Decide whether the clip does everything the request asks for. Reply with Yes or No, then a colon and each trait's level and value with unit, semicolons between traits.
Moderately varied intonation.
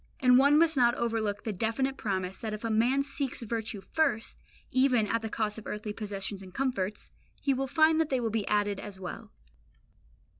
Yes: average, 4.3 semitones